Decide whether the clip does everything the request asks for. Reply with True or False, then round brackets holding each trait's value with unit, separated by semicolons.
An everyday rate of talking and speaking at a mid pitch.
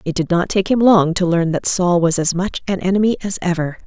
False (265 wpm; 180 Hz)